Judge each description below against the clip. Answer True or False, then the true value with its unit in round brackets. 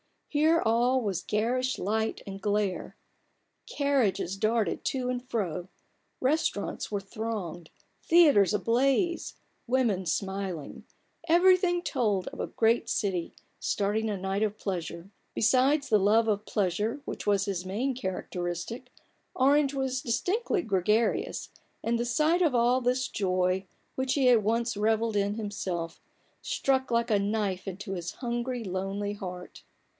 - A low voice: False (220 Hz)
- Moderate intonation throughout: True (4.7 semitones)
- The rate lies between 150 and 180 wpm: False (135 wpm)